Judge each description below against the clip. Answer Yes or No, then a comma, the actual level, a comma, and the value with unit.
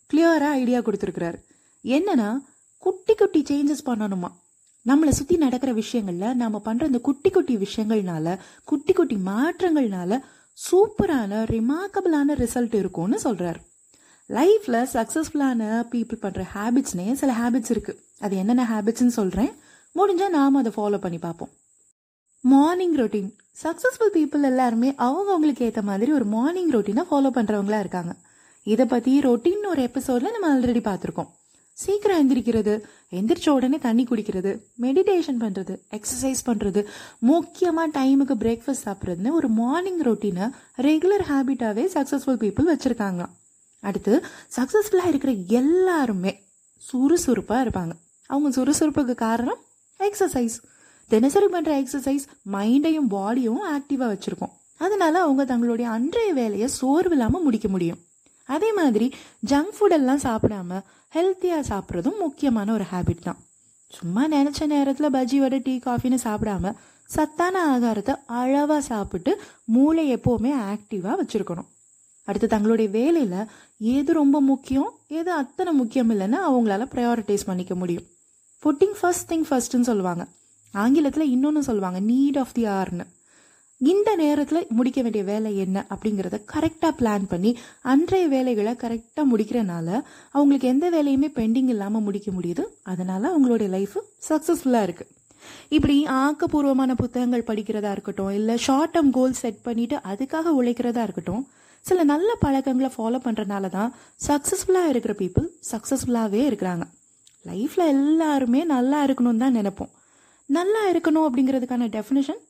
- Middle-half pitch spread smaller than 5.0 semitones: No, wide, 5.5 semitones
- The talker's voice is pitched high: Yes, very high, 255 Hz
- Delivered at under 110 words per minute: No, average, 120 wpm